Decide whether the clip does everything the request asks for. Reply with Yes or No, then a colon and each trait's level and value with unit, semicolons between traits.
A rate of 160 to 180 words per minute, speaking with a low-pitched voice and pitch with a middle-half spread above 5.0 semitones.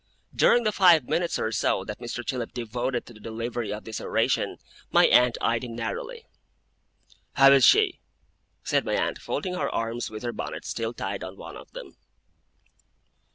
Yes: average, 175 wpm; low, 120 Hz; wide, 5.6 semitones